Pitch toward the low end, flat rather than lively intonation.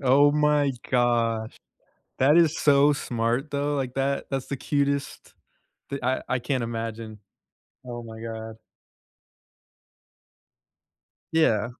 No: low, 130 Hz; average, 3.7 semitones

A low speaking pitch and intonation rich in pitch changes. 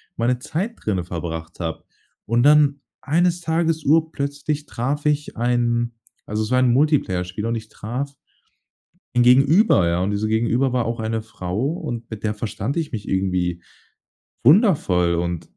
Yes: low, 120 Hz; wide, 6.1 semitones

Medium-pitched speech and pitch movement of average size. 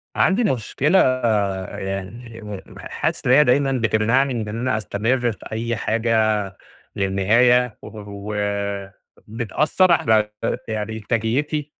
No: low, 115 Hz; average, 3.3 semitones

